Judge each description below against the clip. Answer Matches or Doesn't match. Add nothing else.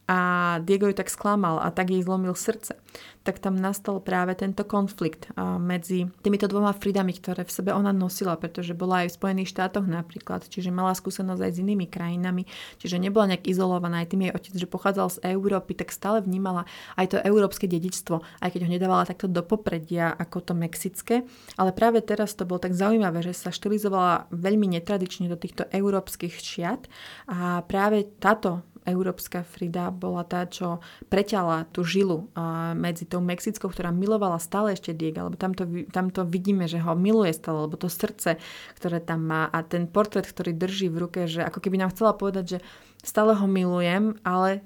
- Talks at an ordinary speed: Doesn't match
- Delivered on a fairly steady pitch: Matches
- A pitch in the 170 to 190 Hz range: Matches